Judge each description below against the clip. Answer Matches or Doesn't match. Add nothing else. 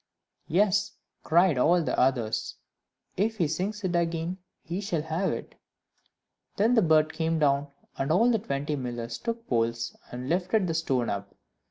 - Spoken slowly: Doesn't match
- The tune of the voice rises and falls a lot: Matches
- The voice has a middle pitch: Matches